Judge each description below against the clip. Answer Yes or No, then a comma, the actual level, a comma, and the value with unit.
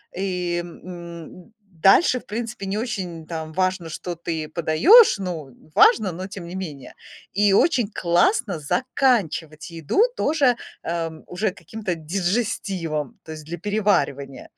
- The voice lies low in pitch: No, medium, 180 Hz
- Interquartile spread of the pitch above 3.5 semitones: Yes, average, 4.2 semitones